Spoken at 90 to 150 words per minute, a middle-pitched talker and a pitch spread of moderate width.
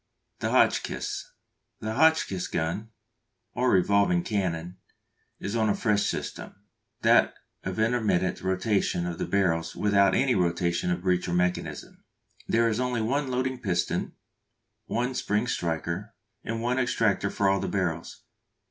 No: average, 140 wpm; low, 100 Hz; average, 4.5 semitones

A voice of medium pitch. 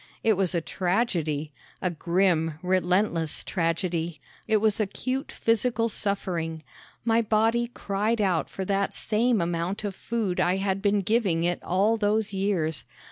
No: high, 195 Hz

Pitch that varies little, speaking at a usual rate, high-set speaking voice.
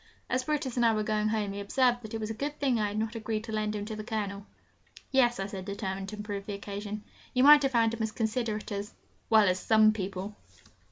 No: narrow, 2.2 semitones; fast, 255 wpm; high, 215 Hz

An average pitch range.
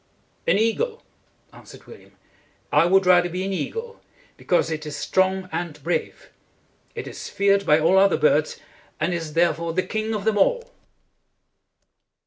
Yes: average, 3.3 semitones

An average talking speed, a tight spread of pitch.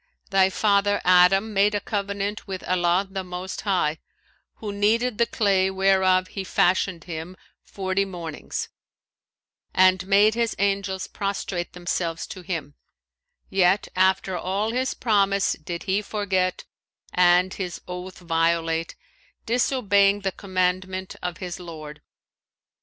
No: slow, 125 wpm; narrow, 2.0 semitones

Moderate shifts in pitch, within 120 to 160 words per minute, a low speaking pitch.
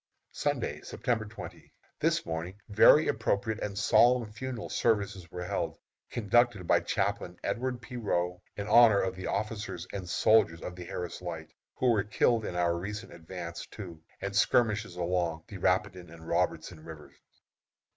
Yes: average, 3.9 semitones; average, 155 wpm; low, 100 Hz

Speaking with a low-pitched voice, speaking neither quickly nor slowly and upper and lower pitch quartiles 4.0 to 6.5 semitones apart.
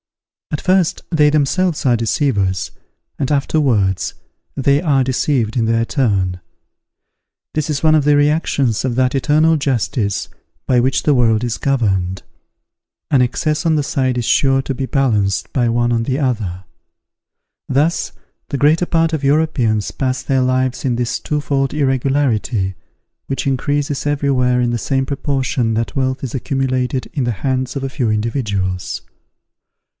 No: low, 130 Hz; average, 150 wpm; average, 3.6 semitones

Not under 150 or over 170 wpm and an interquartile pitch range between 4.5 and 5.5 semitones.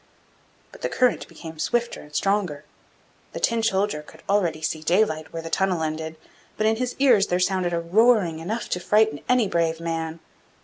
No: average, 180 wpm; average, 5.1 semitones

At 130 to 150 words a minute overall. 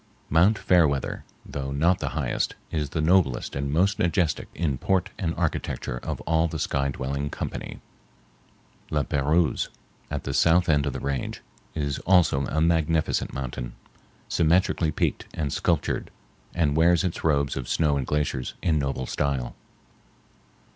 Yes: average, 145 wpm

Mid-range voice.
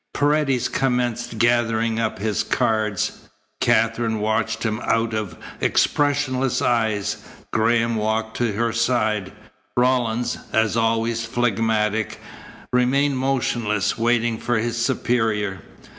No: low, 115 Hz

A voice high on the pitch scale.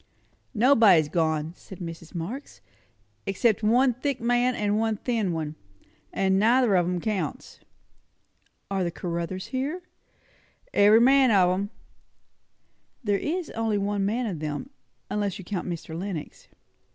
Yes: high, 200 Hz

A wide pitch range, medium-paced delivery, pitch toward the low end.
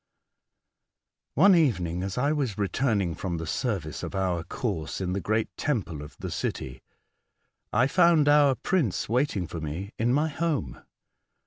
Yes: wide, 8.3 semitones; average, 150 wpm; low, 105 Hz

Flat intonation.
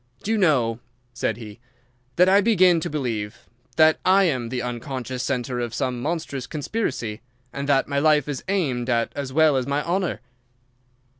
No: average, 4.8 semitones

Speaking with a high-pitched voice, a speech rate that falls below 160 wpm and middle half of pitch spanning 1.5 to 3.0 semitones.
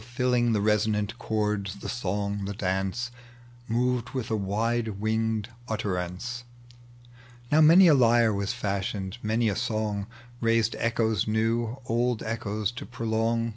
No: low, 110 Hz; slow, 135 wpm; narrow, 2.5 semitones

